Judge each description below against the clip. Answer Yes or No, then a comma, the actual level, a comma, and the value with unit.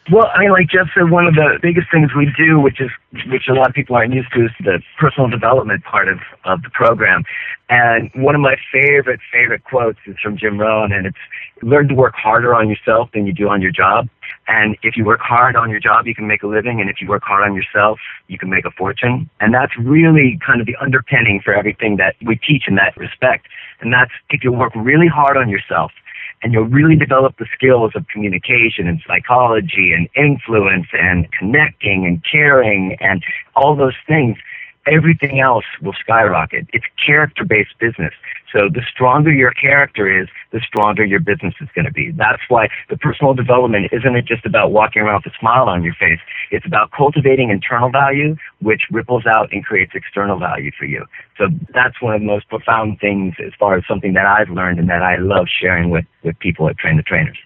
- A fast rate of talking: Yes, fast, 215 wpm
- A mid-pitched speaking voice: No, low, 115 Hz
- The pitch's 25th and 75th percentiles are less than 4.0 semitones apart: No, average, 4.8 semitones